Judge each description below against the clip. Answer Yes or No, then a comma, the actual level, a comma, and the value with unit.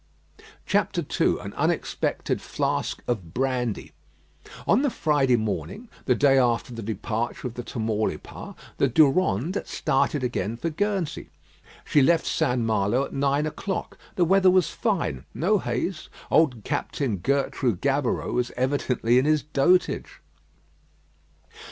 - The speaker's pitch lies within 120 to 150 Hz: Yes, low, 135 Hz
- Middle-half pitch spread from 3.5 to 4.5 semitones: No, average, 4.9 semitones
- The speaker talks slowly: Yes, slow, 125 wpm